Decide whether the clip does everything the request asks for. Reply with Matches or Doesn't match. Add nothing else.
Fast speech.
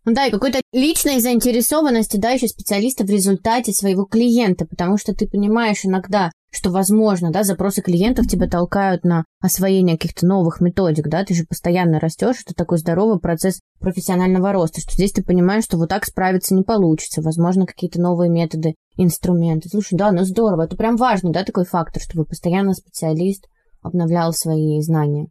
Matches